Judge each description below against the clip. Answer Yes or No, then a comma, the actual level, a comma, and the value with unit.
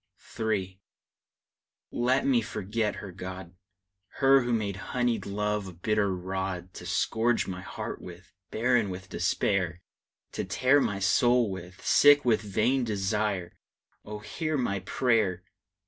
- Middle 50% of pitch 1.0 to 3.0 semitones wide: No, average, 4.2 semitones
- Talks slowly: Yes, slow, 130 wpm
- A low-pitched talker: Yes, low, 105 Hz